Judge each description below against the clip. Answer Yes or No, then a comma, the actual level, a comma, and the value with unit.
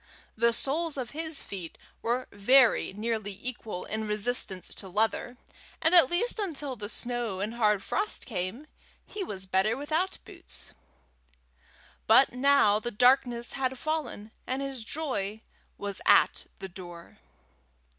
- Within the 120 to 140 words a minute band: Yes, slow, 135 wpm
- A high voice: Yes, high, 235 Hz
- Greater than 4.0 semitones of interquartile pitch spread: Yes, average, 5.0 semitones